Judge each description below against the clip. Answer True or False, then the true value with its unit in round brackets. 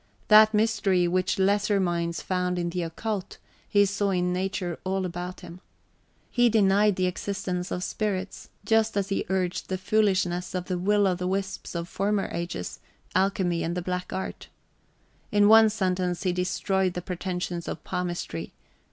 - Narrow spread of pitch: True (2.1 semitones)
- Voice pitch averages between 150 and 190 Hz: True (185 Hz)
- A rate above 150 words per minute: True (160 wpm)